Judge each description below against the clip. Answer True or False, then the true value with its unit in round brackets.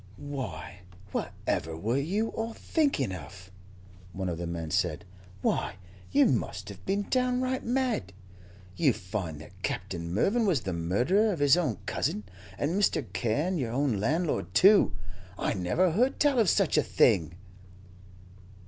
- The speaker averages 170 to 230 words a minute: False (150 wpm)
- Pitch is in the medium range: False (130 Hz)